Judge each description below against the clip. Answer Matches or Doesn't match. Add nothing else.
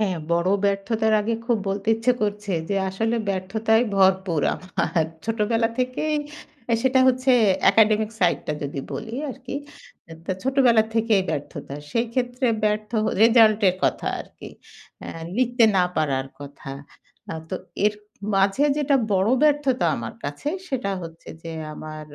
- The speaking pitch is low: Doesn't match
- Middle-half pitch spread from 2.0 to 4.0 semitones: Doesn't match